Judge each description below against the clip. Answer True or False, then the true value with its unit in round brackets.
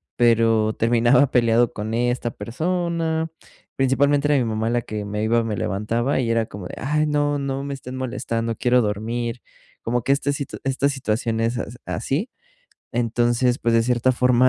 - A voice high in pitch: False (120 Hz)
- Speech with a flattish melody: False (3.2 semitones)